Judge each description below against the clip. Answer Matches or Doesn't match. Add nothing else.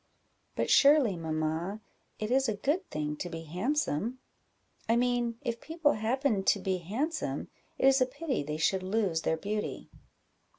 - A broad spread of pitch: Matches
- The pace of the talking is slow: Doesn't match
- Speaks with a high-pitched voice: Matches